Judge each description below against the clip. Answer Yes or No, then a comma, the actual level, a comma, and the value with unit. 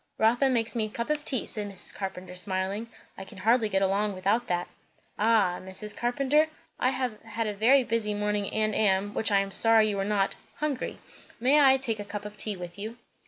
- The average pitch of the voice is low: No, high, 210 Hz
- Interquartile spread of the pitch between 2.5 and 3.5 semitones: Yes, average, 2.9 semitones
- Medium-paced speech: No, fast, 210 wpm